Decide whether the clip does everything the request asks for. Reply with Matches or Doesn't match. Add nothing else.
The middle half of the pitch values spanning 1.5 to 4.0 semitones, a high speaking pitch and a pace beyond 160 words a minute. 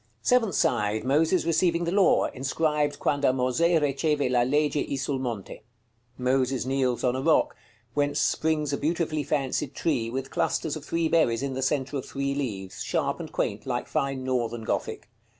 Doesn't match